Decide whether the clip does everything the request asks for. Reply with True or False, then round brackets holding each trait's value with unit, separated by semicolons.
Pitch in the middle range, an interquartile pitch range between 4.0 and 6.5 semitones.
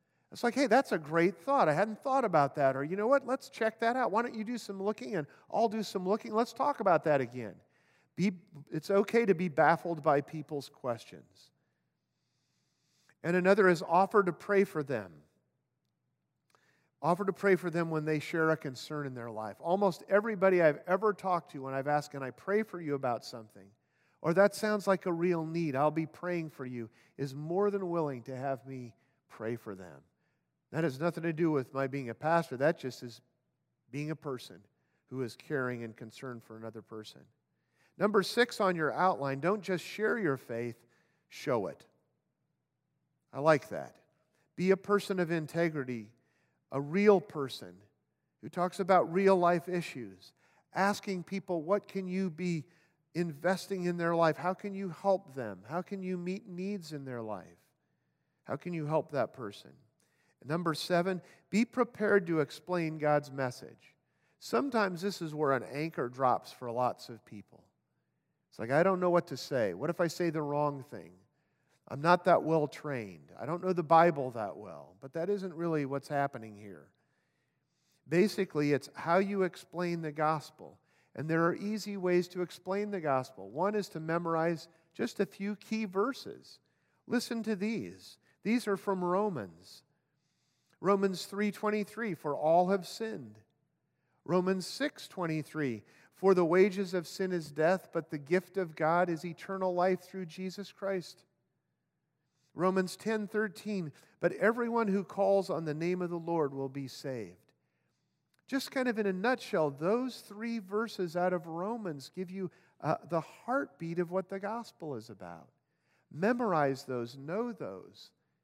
True (170 Hz; 5.5 semitones)